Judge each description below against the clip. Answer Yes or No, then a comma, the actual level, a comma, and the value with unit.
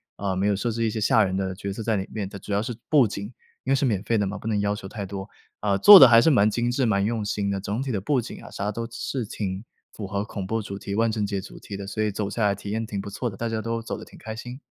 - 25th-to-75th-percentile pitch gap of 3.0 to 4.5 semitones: No, narrow, 2.6 semitones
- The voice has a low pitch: Yes, low, 105 Hz